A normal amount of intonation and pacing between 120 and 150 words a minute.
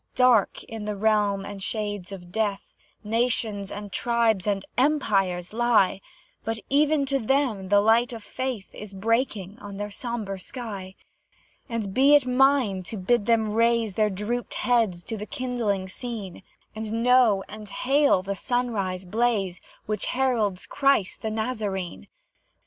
Yes: average, 3.6 semitones; average, 145 wpm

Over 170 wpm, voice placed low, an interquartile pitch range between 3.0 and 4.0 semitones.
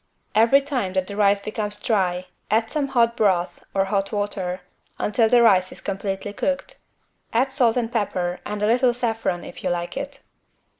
No: average, 180 wpm; high, 210 Hz; average, 3.7 semitones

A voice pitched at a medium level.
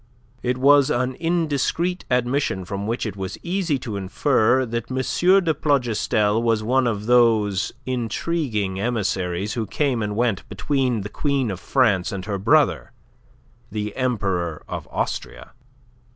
No: low, 120 Hz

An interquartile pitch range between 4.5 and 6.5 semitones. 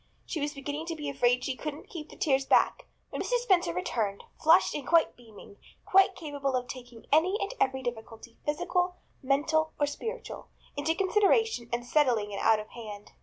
Yes: average, 5.1 semitones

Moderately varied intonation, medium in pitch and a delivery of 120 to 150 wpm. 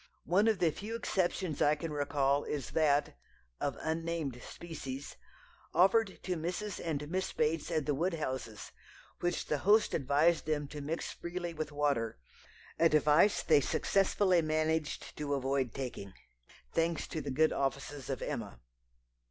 Yes: average, 3.3 semitones; medium, 155 Hz; average, 145 wpm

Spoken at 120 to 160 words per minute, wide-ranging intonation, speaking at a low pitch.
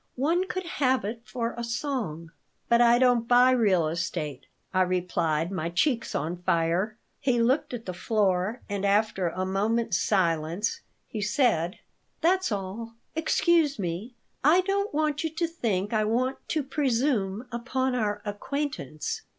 No: average, 150 wpm; wide, 6.0 semitones; high, 225 Hz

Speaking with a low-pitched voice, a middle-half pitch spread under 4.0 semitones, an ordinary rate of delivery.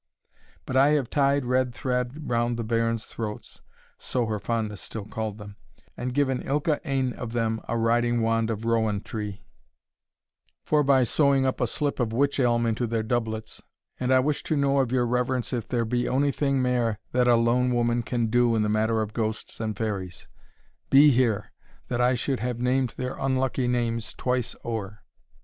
Yes: low, 120 Hz; narrow, 2.4 semitones; average, 185 wpm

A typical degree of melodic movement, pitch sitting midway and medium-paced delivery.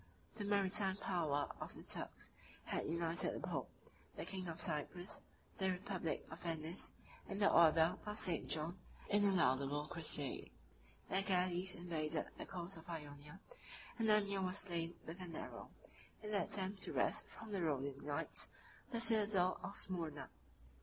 Yes: average, 3.4 semitones; medium, 175 Hz; average, 160 wpm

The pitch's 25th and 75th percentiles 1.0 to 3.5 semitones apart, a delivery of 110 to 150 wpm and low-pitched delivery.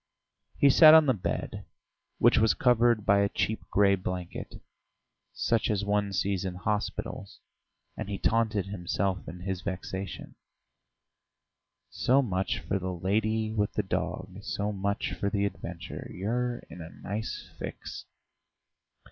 Yes: average, 2.7 semitones; average, 140 wpm; low, 100 Hz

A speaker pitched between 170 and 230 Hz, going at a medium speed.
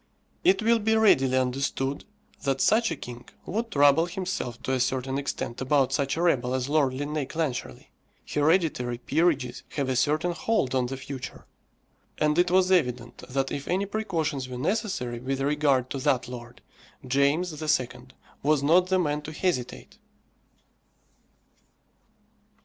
No: medium, 140 Hz; average, 150 wpm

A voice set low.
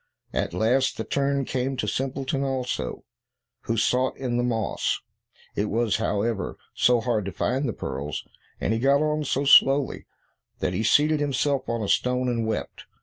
Yes: low, 125 Hz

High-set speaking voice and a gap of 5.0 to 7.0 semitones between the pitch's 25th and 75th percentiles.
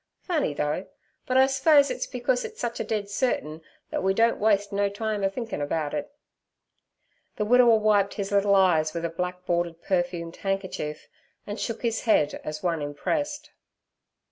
Yes: high, 200 Hz; wide, 5.4 semitones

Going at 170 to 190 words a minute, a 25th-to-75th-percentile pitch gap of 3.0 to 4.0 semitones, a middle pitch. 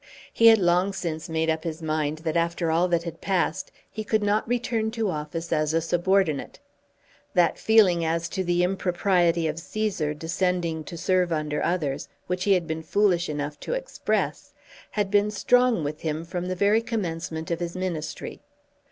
Yes: average, 180 wpm; average, 3.4 semitones; medium, 175 Hz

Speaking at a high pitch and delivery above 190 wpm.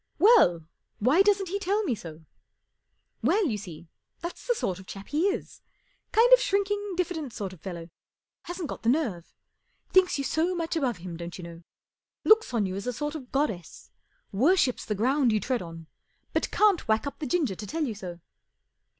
Yes: very high, 265 Hz; average, 200 wpm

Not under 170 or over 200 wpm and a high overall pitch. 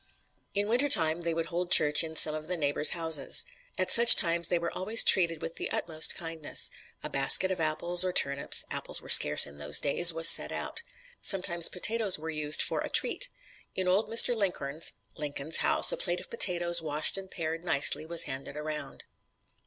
No: average, 190 wpm; medium, 165 Hz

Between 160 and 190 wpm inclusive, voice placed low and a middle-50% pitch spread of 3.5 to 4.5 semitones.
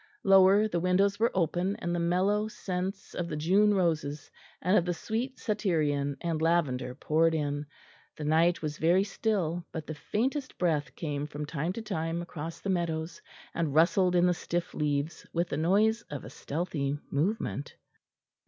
No: average, 170 wpm; medium, 170 Hz; average, 3.8 semitones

